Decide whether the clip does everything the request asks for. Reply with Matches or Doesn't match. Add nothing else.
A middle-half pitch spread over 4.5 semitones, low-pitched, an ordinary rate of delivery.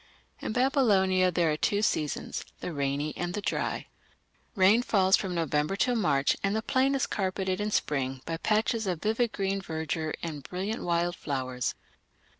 Doesn't match